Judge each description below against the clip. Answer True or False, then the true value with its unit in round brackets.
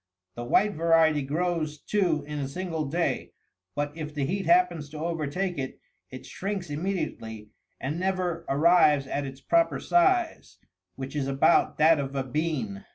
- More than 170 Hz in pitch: False (155 Hz)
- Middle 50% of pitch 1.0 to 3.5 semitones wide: False (4.3 semitones)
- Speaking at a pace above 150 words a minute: True (160 wpm)